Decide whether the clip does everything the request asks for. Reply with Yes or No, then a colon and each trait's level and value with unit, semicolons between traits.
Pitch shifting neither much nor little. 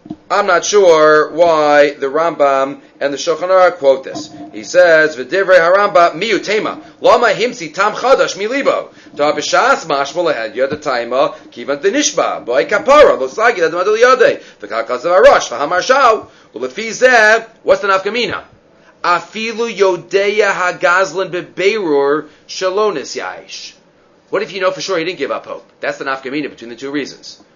No: wide, 5.8 semitones